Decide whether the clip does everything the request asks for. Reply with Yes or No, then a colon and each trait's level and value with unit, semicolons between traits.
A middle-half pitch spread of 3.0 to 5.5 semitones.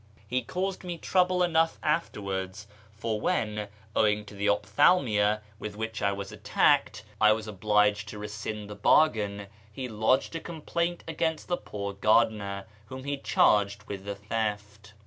Yes: average, 5.0 semitones